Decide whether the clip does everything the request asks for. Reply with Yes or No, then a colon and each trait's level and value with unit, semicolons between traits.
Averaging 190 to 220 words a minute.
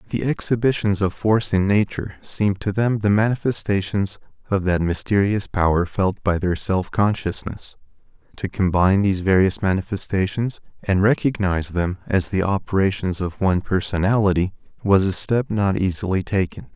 No: average, 145 wpm